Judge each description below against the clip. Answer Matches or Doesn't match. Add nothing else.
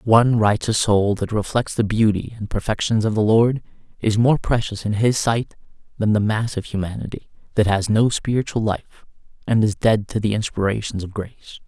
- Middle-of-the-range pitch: Doesn't match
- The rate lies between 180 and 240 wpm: Matches